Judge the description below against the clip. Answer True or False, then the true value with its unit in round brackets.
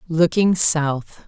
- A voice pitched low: False (160 Hz)